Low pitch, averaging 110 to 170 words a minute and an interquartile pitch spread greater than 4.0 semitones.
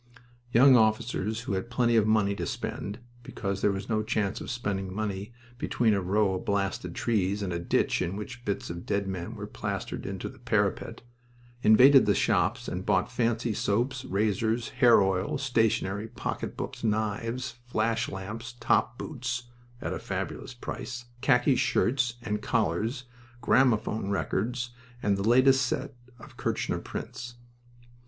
No: low, 110 Hz; average, 150 wpm; average, 3.3 semitones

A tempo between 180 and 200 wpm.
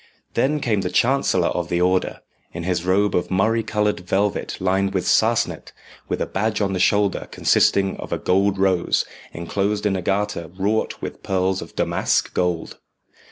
No: average, 170 wpm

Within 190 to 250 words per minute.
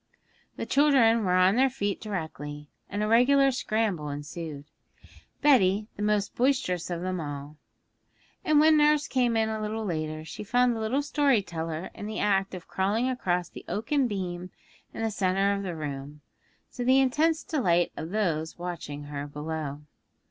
No: average, 170 wpm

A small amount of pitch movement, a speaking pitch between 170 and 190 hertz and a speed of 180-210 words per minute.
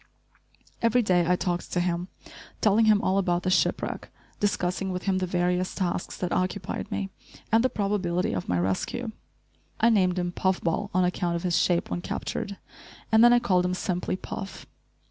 Yes: narrow, 2.3 semitones; medium, 185 Hz; average, 185 wpm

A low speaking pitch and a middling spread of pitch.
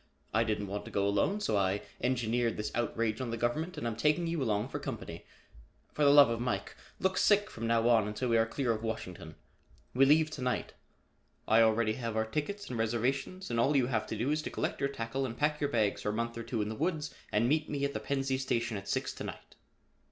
Yes: low, 120 Hz; average, 4.2 semitones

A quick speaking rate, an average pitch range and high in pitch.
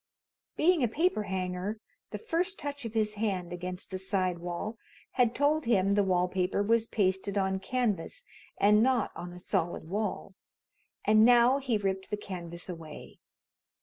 No: average, 160 wpm; average, 4.4 semitones; high, 205 Hz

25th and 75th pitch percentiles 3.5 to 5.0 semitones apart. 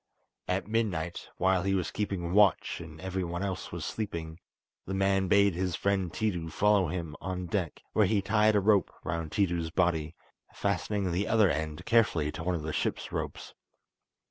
No: average, 3.0 semitones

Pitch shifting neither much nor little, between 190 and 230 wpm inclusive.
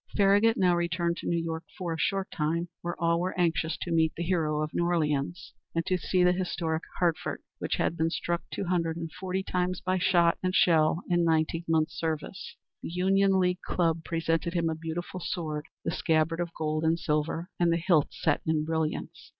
No: narrow, 1.8 semitones; average, 200 wpm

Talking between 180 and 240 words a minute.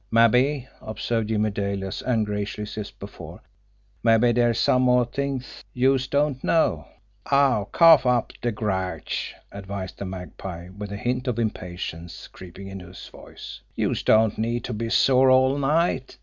No: average, 150 wpm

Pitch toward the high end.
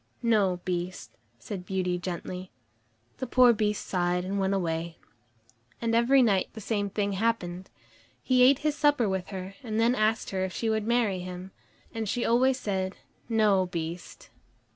Yes: high, 200 Hz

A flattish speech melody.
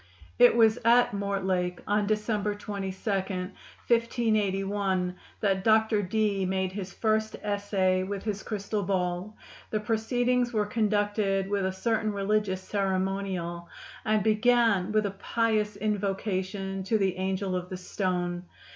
Yes: narrow, 2.2 semitones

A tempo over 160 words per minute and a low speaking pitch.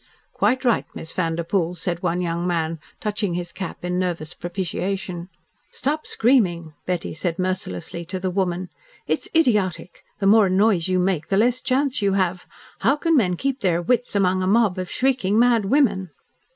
No: average, 170 wpm; medium, 185 Hz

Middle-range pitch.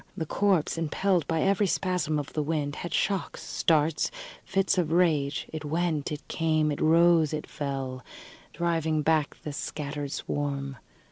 Yes: medium, 155 Hz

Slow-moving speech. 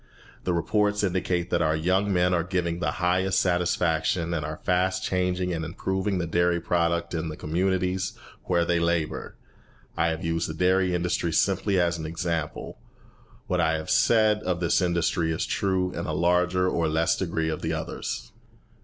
No: average, 175 wpm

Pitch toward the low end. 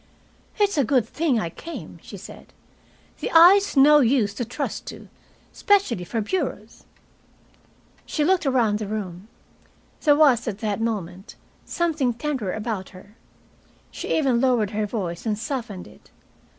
No: high, 235 Hz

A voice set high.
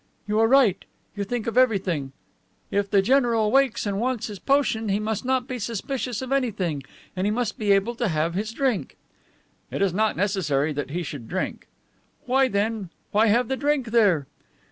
Yes: high, 215 Hz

